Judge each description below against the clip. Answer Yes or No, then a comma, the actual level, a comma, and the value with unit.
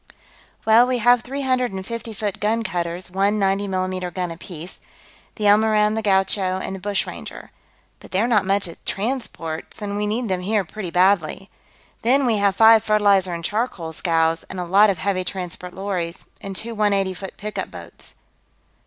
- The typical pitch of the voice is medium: No, high, 200 Hz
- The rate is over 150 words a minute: Yes, average, 180 wpm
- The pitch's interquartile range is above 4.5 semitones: No, average, 2.7 semitones